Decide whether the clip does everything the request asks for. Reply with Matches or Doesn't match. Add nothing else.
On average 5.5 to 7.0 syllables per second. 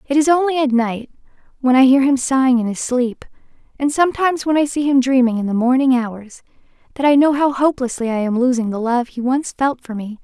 Matches